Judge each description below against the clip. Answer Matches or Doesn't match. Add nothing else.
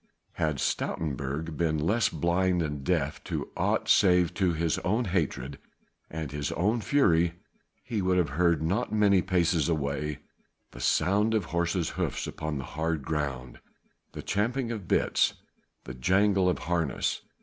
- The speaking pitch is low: Matches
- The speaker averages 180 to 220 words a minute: Doesn't match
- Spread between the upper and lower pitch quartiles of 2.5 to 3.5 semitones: Doesn't match